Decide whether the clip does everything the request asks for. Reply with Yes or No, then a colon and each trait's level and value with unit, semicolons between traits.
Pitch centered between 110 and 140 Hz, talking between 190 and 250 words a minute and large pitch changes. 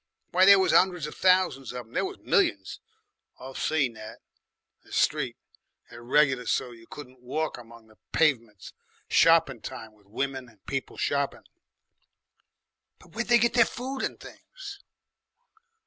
No: low, 135 Hz; average, 150 wpm; wide, 7.6 semitones